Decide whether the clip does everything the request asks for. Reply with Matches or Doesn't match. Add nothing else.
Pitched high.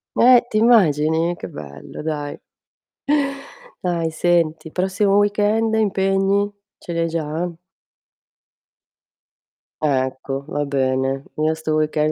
Doesn't match